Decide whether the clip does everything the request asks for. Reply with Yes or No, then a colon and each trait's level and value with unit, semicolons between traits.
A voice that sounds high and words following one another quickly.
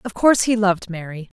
Yes: high, 200 Hz; fast, 215 wpm